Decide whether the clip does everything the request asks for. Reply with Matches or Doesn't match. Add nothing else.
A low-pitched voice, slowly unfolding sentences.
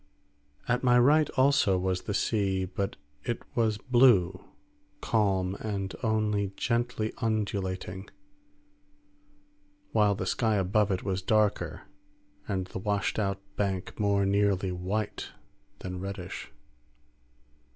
Matches